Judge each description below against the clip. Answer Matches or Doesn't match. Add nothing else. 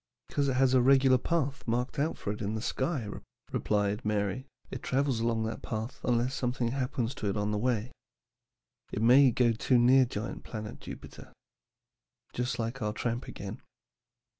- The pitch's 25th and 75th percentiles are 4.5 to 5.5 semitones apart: Doesn't match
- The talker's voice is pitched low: Matches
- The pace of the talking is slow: Doesn't match